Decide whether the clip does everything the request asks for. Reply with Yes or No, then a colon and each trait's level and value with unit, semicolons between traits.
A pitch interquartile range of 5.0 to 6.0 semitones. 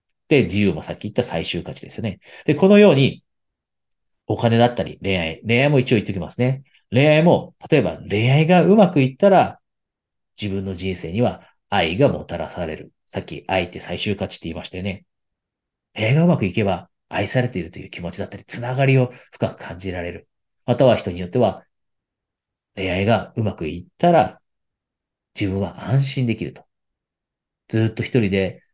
Yes: wide, 5.4 semitones